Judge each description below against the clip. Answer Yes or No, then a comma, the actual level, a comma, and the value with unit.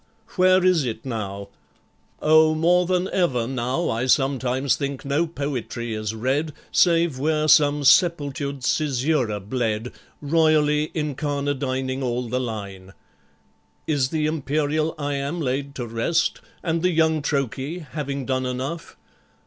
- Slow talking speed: Yes, slow, 125 wpm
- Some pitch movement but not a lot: Yes, average, 3.6 semitones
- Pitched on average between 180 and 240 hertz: No, medium, 140 Hz